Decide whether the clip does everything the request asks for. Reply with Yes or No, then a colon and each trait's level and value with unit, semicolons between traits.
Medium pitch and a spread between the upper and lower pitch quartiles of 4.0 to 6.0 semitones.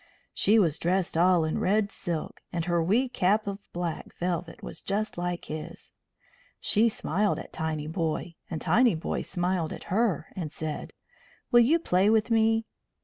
Yes: medium, 180 Hz; average, 4.6 semitones